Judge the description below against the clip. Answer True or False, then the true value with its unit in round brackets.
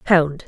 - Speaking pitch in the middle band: True (165 Hz)